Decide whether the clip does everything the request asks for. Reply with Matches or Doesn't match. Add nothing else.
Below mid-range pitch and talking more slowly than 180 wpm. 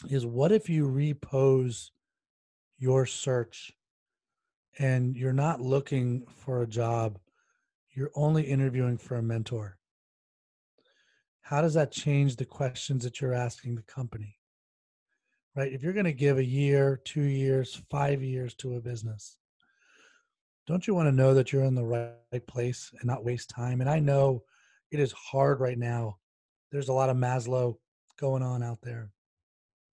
Matches